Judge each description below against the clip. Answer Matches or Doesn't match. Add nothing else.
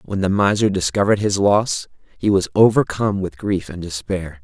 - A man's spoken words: Matches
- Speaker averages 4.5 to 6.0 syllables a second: Matches